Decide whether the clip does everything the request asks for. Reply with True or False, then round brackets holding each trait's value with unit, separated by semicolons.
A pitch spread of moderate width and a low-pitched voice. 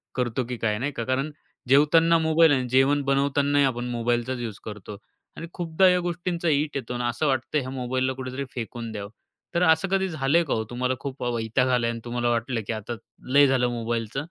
True (3.5 semitones; 130 Hz)